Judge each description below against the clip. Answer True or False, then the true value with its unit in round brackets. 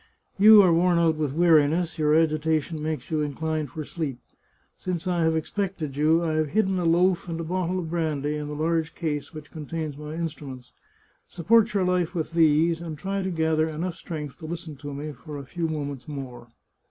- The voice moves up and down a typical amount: False (2.3 semitones)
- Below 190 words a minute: False (200 wpm)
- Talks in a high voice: False (160 Hz)